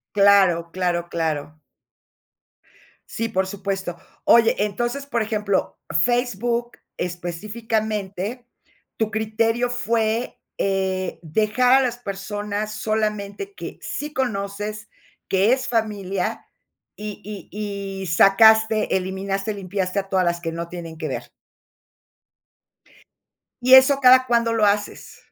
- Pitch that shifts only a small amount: No, average, 3.2 semitones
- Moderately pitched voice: No, high, 210 Hz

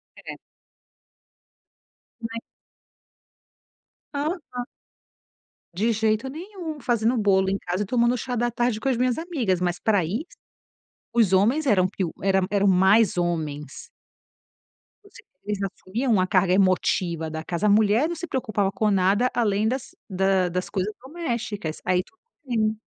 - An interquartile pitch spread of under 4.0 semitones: No, average, 4.6 semitones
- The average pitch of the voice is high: Yes, high, 210 Hz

